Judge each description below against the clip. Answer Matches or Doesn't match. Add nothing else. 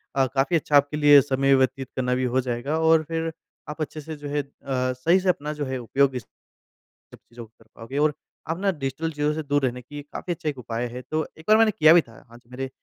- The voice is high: Doesn't match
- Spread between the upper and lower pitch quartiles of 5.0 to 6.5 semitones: Doesn't match